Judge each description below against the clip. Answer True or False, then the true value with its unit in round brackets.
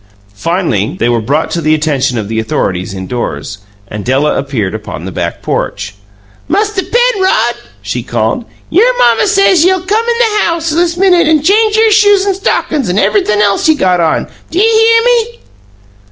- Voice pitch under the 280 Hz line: False (310 Hz)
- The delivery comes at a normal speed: True (175 wpm)